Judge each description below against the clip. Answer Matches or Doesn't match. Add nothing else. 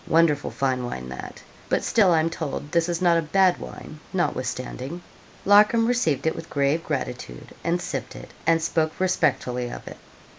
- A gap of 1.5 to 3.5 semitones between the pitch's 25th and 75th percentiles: Doesn't match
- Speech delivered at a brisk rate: Doesn't match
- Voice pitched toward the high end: Doesn't match